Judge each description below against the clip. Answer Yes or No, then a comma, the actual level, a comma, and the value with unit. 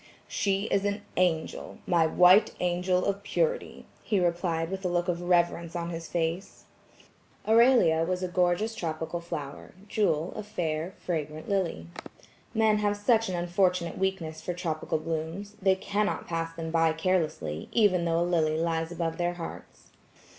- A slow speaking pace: No, average, 155 wpm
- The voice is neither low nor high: Yes, medium, 175 Hz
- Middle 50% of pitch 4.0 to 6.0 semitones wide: No, average, 2.8 semitones